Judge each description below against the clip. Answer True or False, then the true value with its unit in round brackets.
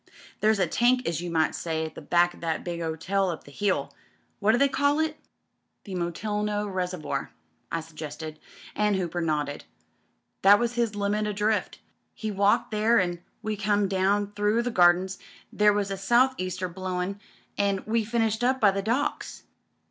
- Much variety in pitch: False (3.5 semitones)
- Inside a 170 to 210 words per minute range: True (190 wpm)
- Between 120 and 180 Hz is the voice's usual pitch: False (200 Hz)